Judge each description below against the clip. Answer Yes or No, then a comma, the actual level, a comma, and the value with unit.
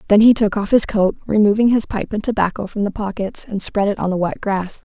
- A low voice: No, high, 205 Hz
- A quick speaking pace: Yes, fast, 255 wpm